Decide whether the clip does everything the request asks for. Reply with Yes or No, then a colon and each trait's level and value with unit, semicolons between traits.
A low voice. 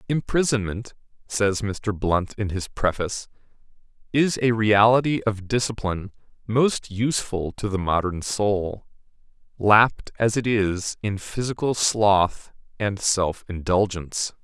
Yes: low, 105 Hz